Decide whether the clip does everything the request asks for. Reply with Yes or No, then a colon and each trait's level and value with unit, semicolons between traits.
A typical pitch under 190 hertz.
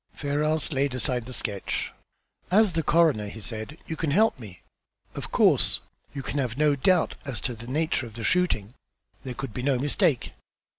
Yes: low, 135 Hz